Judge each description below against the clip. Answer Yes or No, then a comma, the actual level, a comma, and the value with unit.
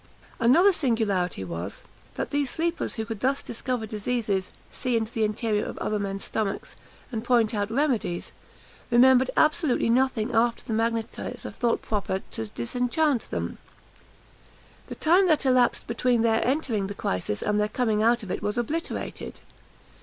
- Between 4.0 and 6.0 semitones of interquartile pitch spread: No, average, 3.3 semitones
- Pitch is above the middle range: Yes, high, 230 Hz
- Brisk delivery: No, average, 155 wpm